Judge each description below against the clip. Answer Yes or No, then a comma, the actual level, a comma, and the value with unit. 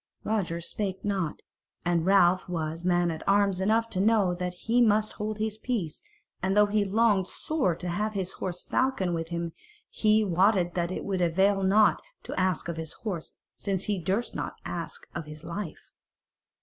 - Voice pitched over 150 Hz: Yes, high, 190 Hz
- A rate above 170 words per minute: Yes, average, 180 wpm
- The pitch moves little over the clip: No, average, 3.3 semitones